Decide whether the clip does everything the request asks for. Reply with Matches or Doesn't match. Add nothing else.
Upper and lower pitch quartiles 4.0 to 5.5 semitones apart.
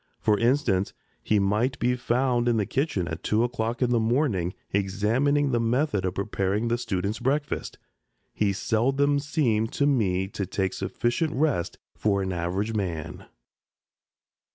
Matches